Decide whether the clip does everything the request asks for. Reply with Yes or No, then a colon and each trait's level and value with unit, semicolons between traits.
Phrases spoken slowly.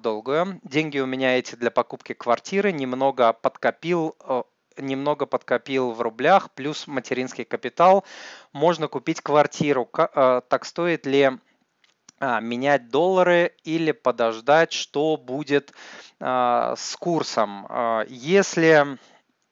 Yes: slow, 100 wpm